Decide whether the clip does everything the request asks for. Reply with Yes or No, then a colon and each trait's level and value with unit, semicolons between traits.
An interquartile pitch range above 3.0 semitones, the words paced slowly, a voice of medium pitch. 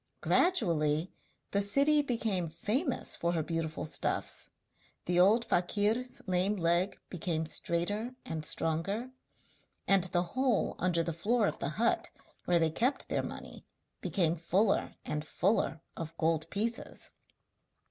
Yes: average, 5.1 semitones; slow, 130 wpm; medium, 180 Hz